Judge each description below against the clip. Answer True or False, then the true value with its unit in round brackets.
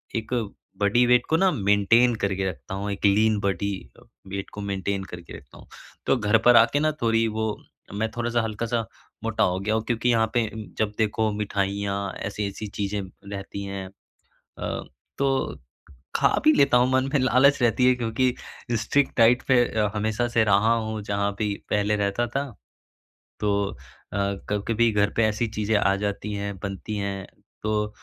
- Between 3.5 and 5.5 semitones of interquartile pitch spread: False (2.7 semitones)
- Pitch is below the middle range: True (105 Hz)